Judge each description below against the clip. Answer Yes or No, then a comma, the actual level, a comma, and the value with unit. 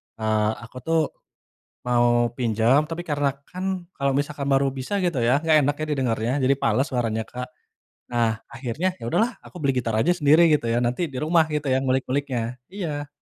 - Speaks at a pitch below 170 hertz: Yes, low, 135 Hz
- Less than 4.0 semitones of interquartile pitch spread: No, average, 4.3 semitones